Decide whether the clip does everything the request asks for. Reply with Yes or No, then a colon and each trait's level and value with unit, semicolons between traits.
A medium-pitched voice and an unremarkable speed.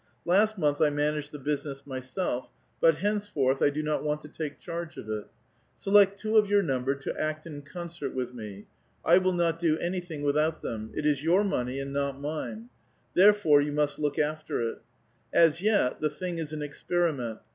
Yes: medium, 150 Hz; average, 190 wpm